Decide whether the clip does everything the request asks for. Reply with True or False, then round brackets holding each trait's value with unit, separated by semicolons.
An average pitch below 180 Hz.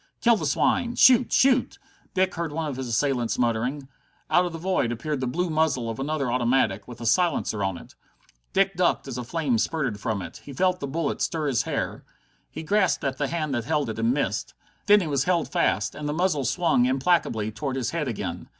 True (140 Hz)